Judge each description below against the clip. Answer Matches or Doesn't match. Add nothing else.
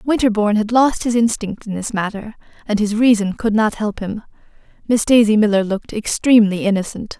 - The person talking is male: Doesn't match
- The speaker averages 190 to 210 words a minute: Doesn't match